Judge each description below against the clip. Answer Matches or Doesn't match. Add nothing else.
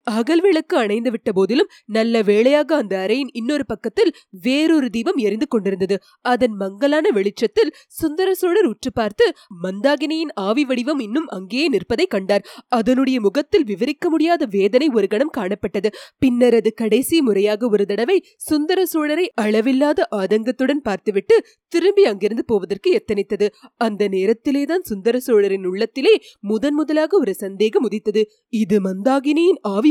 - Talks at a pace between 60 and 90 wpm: Doesn't match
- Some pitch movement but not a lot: Doesn't match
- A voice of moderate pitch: Doesn't match